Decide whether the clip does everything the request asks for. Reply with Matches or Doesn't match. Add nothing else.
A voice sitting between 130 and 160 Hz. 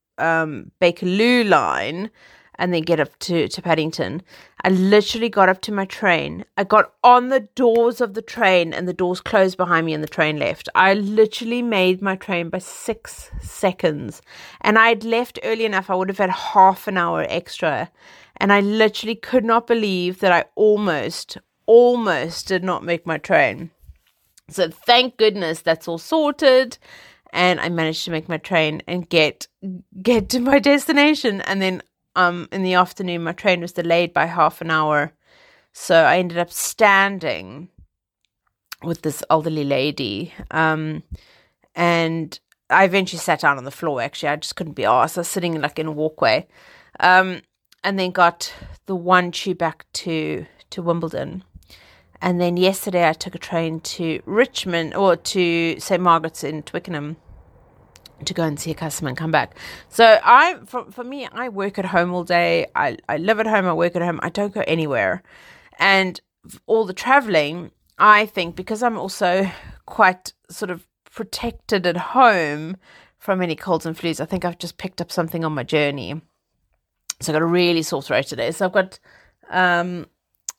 Doesn't match